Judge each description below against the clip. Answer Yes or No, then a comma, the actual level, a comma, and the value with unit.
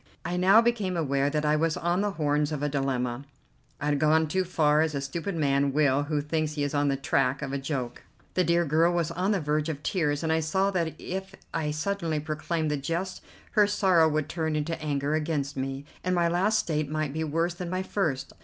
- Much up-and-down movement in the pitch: No, average, 3.0 semitones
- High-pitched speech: No, medium, 155 Hz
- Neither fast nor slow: No, fast, 230 wpm